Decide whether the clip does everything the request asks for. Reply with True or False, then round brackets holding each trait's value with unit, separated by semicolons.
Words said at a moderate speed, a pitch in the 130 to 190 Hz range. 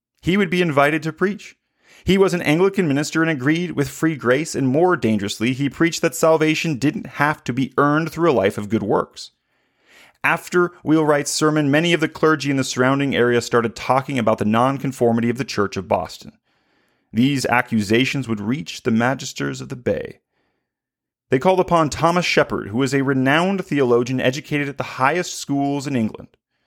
True (180 wpm; 140 Hz)